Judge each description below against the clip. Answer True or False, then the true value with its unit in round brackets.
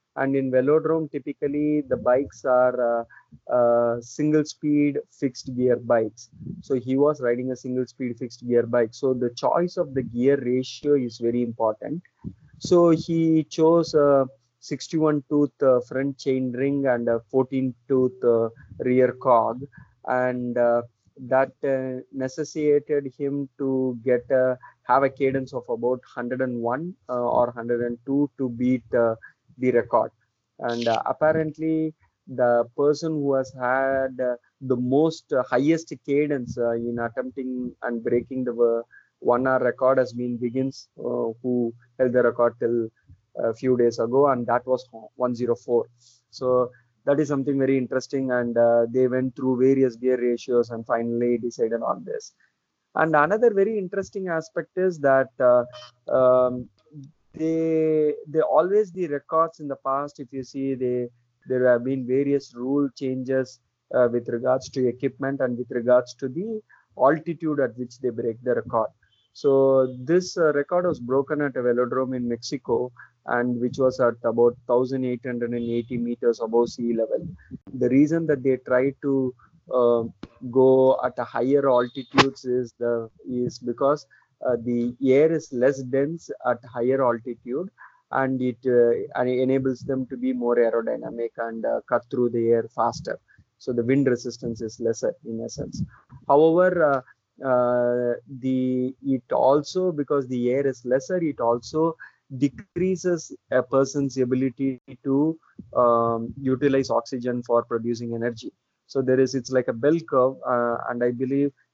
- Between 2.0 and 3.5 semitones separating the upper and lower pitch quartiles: True (2.7 semitones)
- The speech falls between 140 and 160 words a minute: True (155 wpm)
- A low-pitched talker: True (130 Hz)